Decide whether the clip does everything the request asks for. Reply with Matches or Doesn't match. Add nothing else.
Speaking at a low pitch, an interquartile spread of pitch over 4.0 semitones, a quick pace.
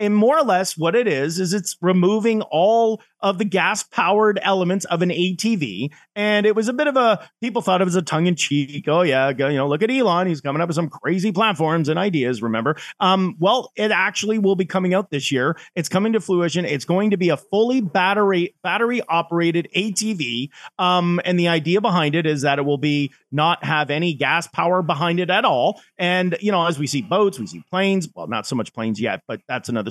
Doesn't match